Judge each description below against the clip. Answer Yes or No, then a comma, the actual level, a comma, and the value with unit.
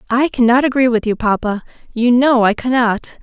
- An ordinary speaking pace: Yes, average, 185 wpm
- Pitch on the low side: No, high, 240 Hz